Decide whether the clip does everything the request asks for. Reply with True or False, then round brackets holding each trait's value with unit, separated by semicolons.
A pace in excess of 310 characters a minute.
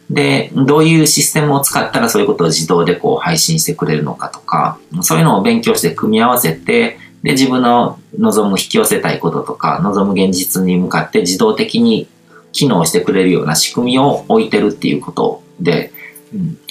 True (390 characters per minute)